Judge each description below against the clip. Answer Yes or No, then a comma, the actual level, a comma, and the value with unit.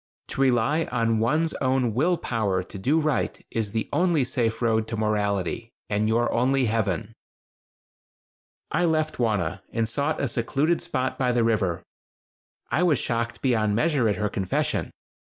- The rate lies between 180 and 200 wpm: No, average, 155 wpm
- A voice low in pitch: Yes, low, 115 Hz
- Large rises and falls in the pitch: No, average, 4.2 semitones